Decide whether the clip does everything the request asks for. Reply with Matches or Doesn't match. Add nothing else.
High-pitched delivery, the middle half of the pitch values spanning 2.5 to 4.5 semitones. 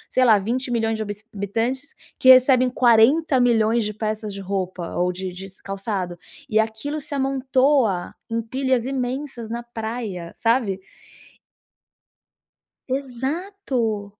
Matches